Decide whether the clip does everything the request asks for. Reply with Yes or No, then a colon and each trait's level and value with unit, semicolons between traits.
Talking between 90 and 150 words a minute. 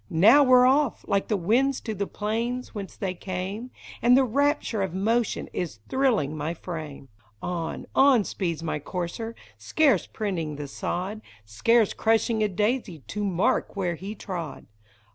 No: average, 160 wpm